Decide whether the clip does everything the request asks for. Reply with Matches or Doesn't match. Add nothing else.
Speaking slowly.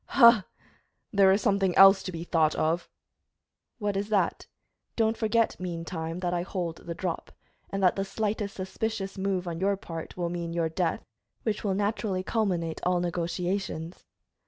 Doesn't match